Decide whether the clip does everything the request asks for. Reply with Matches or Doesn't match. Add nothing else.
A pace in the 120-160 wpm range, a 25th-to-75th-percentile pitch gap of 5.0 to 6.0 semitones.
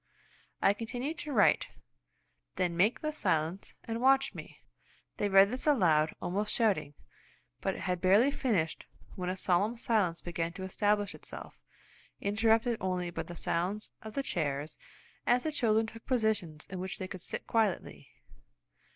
Doesn't match